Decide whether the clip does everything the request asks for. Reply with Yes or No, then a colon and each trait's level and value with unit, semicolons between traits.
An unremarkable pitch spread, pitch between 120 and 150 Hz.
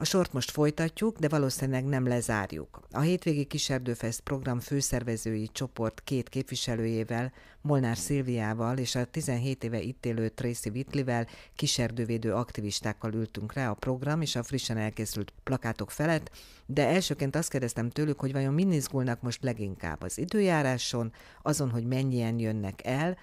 Yes: average, 3.7 semitones; low, 125 Hz